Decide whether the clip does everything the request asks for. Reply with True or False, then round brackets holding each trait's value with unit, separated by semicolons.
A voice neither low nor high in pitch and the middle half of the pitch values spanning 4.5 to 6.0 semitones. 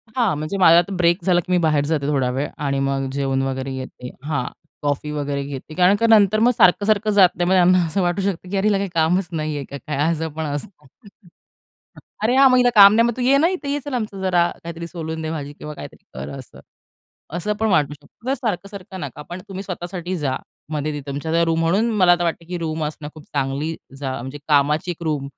True (165 Hz; 4.8 semitones)